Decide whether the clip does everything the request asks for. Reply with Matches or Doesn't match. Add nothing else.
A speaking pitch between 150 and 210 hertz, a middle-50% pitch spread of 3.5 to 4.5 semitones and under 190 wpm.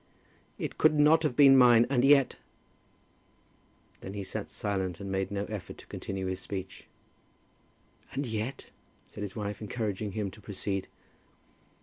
Doesn't match